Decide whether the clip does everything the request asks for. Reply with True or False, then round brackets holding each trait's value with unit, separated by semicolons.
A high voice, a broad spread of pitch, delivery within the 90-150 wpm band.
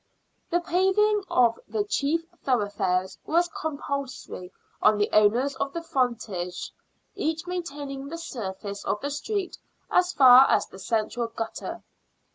True (275 Hz; 7.7 semitones; 135 wpm)